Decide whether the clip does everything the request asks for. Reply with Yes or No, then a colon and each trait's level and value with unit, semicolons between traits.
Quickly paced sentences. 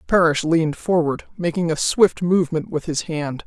No: average, 175 wpm